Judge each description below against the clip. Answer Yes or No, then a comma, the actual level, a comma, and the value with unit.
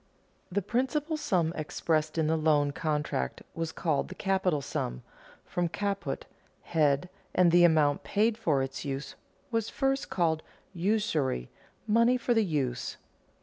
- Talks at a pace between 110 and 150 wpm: Yes, average, 140 wpm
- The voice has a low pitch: No, medium, 165 Hz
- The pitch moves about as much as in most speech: No, wide, 5.7 semitones